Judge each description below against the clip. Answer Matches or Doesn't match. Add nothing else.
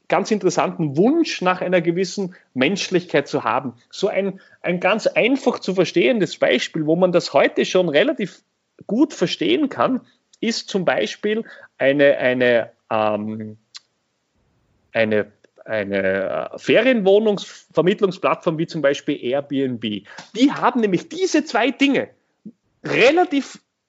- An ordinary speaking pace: Doesn't match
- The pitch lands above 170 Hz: Matches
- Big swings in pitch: Matches